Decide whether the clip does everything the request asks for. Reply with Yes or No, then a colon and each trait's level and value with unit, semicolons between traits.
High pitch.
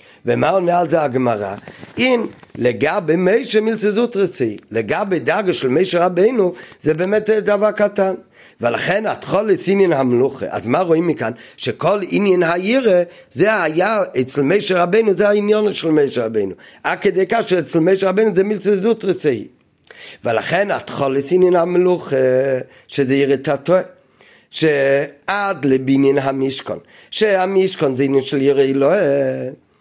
No: medium, 175 Hz